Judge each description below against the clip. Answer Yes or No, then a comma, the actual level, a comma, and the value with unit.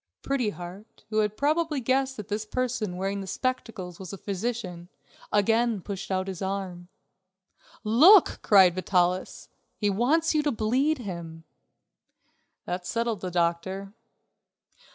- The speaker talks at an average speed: No, slow, 130 wpm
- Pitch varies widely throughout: No, average, 4.7 semitones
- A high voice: Yes, high, 205 Hz